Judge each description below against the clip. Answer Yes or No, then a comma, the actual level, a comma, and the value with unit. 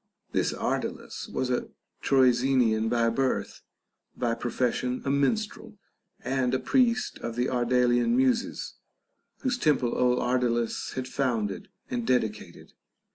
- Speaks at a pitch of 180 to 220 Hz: No, low, 125 Hz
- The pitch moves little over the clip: Yes, narrow, 2.3 semitones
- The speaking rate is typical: No, slow, 125 wpm